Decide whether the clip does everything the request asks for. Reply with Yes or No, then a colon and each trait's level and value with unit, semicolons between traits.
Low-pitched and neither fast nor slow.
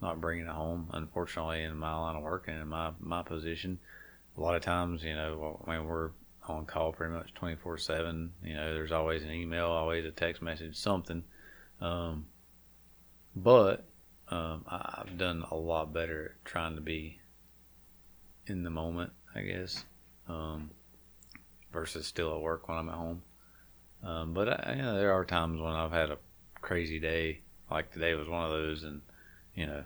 Yes: very low, 80 Hz; average, 180 wpm